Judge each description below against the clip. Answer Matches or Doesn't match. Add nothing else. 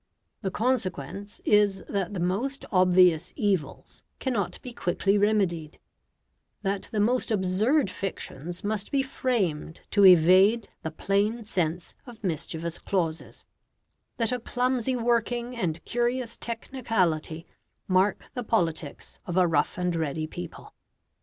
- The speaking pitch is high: Matches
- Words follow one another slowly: Matches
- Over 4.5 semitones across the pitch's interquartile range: Matches